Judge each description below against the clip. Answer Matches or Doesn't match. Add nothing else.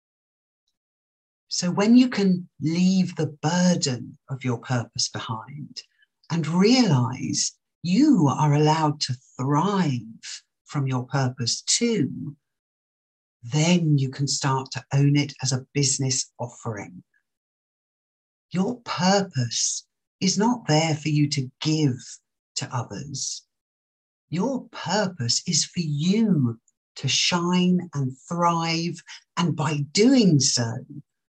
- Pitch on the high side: Doesn't match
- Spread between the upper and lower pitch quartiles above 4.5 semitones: Matches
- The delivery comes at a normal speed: Doesn't match